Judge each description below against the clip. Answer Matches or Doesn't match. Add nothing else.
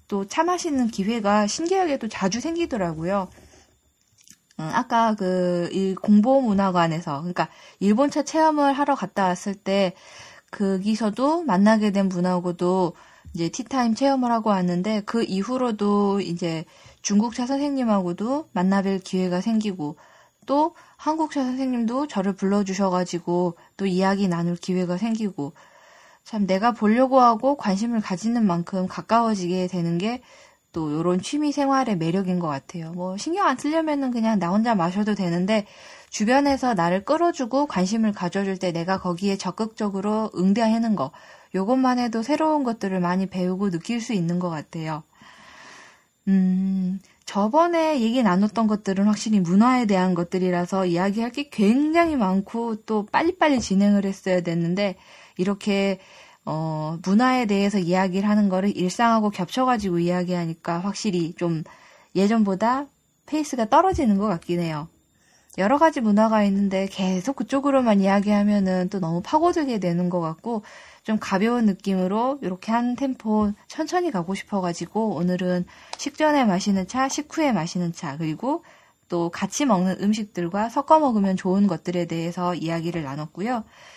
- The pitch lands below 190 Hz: Doesn't match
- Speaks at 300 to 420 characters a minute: Matches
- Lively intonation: Doesn't match